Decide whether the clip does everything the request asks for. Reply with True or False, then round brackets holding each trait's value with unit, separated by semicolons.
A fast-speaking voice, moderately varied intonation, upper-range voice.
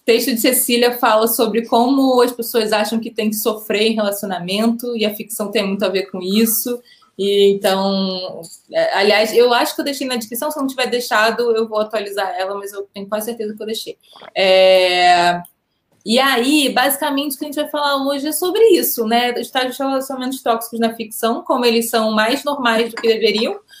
True (200 wpm; 3.3 semitones; 230 Hz)